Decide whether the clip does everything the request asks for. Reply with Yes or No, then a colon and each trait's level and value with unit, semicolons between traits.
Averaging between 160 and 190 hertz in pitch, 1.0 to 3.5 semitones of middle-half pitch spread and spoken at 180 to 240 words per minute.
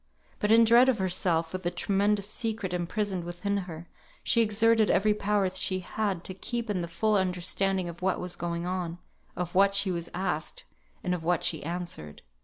Yes: medium, 185 Hz; average, 3.1 semitones; average, 195 wpm